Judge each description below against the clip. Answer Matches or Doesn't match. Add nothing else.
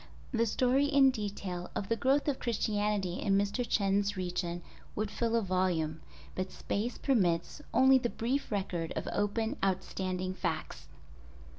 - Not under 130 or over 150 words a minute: Matches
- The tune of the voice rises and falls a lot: Doesn't match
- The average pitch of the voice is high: Matches